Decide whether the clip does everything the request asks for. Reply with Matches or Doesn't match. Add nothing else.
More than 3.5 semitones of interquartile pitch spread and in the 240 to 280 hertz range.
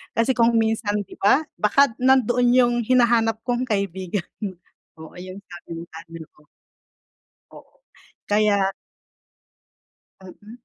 Doesn't match